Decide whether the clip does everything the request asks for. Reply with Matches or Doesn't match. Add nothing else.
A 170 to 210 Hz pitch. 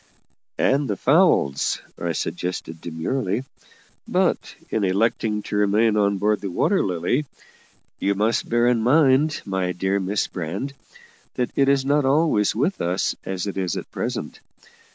Doesn't match